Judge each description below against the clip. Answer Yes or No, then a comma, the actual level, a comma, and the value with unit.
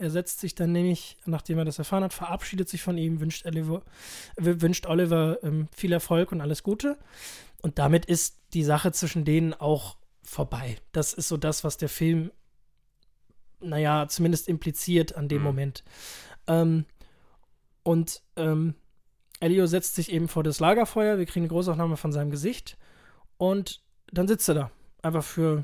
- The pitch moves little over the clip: Yes, narrow, 2.2 semitones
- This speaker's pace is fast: No, average, 165 wpm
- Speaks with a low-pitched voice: No, medium, 165 Hz